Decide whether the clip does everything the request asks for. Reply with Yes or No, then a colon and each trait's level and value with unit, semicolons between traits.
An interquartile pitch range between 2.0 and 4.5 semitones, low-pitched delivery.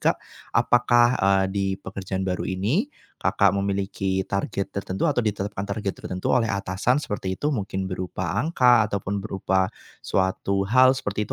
Yes: average, 3.0 semitones; low, 100 Hz